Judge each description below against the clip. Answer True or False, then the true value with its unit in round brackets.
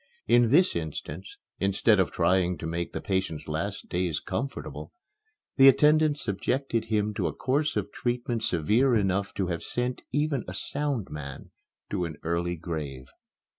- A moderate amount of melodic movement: False (6.4 semitones)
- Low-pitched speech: True (100 Hz)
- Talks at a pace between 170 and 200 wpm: False (155 wpm)